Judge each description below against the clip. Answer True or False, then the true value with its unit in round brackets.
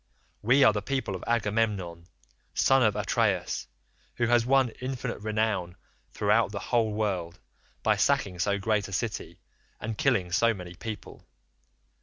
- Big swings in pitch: False (3.3 semitones)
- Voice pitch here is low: True (110 Hz)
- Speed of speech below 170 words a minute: True (145 wpm)